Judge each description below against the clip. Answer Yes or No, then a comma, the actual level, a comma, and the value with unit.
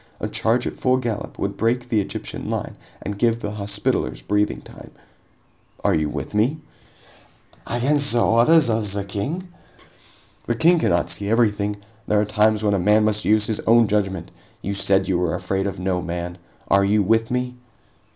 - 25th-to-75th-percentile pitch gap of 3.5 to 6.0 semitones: No, average, 3.0 semitones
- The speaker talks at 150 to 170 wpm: No, average, 180 wpm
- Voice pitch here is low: Yes, low, 105 Hz